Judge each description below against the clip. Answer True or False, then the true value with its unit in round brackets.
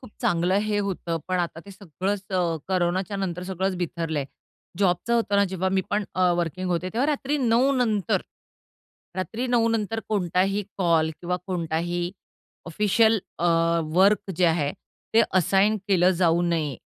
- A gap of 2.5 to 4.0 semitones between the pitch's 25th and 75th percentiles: True (3.1 semitones)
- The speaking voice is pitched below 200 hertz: True (185 Hz)